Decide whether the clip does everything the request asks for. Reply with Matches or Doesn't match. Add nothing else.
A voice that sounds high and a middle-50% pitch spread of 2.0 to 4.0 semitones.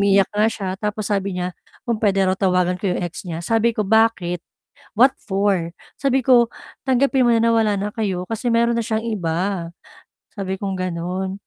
Matches